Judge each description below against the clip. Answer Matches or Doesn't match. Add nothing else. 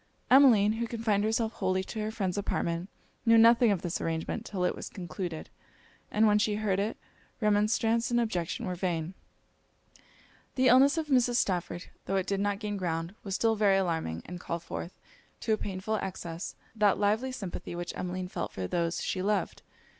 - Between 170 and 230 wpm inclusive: Matches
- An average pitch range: Matches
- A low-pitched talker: Doesn't match